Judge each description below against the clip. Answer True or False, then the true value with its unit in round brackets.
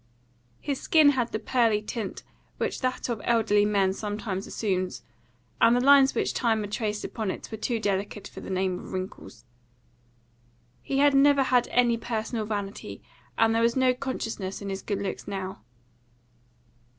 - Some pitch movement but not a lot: True (3.7 semitones)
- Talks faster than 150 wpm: True (165 wpm)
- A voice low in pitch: False (220 Hz)